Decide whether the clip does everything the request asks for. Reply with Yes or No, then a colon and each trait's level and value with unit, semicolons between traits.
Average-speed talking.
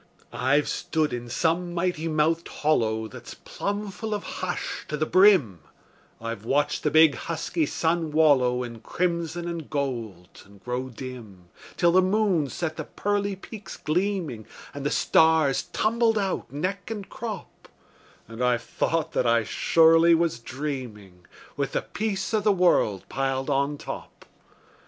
Yes: average, 150 wpm